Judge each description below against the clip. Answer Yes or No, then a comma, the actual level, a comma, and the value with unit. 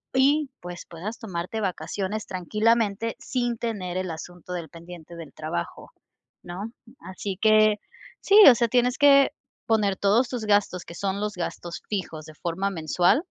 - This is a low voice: No, high, 200 Hz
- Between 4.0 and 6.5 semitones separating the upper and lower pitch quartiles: Yes, average, 4.4 semitones